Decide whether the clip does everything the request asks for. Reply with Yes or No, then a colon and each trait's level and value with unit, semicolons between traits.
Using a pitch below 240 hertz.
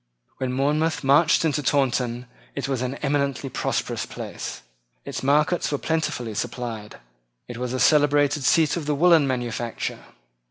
Yes: medium, 140 Hz